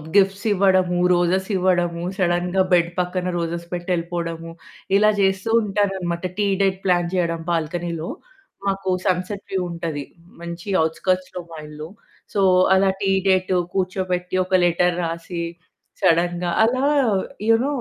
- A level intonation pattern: Yes, narrow, 1.9 semitones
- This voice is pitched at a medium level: Yes, medium, 180 Hz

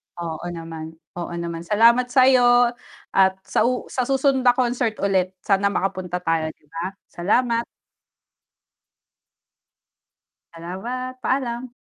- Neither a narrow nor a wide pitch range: No, wide, 6.3 semitones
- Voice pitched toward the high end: Yes, high, 210 Hz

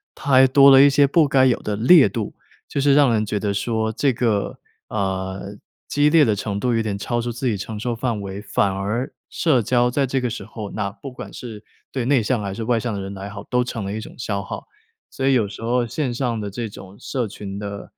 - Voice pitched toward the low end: Yes, low, 115 Hz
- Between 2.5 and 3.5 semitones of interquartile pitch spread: No, average, 4.1 semitones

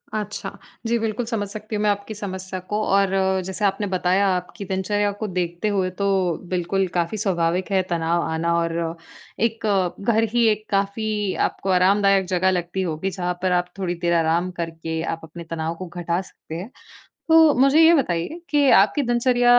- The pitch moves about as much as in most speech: Yes, average, 3.3 semitones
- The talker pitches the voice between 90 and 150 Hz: No, high, 190 Hz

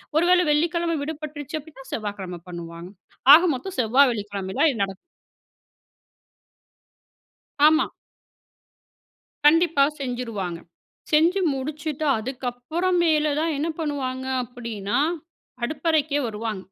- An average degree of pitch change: No, wide, 6.1 semitones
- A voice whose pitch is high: Yes, very high, 275 Hz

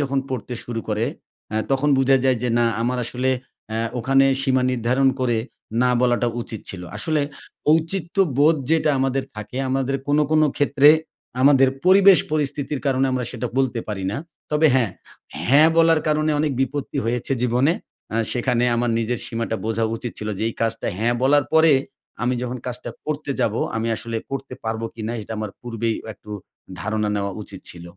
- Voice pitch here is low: Yes, low, 125 Hz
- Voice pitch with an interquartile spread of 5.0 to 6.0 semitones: No, average, 3.8 semitones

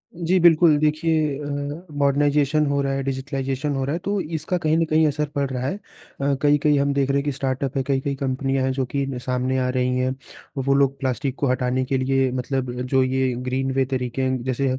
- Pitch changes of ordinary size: No, narrow, 1.9 semitones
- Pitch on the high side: No, low, 135 Hz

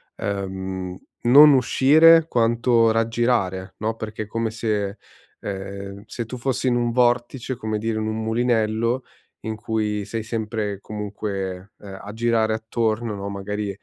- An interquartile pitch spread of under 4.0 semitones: Yes, narrow, 2.6 semitones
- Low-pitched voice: Yes, low, 110 Hz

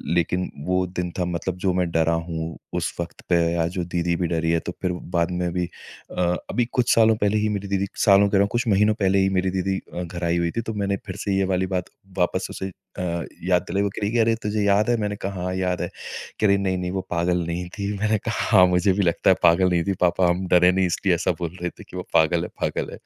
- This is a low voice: Yes, very low, 90 Hz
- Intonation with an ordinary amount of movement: No, narrow, 2.3 semitones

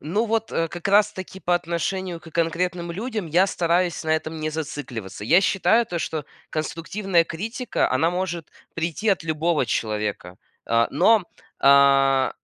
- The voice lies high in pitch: No, medium, 170 Hz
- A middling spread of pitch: Yes, average, 3.7 semitones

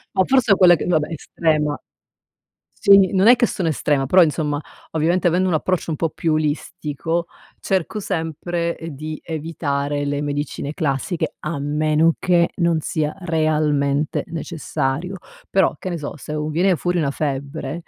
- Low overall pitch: No, medium, 160 Hz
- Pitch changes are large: No, average, 2.9 semitones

